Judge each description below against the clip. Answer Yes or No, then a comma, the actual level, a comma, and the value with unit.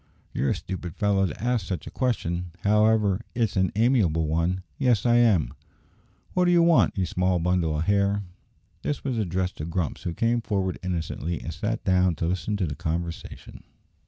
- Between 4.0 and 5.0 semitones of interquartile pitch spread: Yes, average, 4.4 semitones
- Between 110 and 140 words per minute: No, average, 185 wpm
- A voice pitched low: Yes, very low, 95 Hz